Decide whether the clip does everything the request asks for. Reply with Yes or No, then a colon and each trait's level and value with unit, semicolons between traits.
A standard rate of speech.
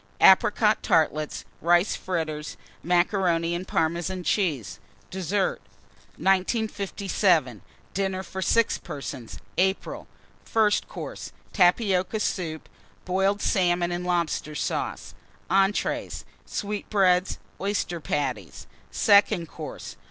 No: slow, 90 wpm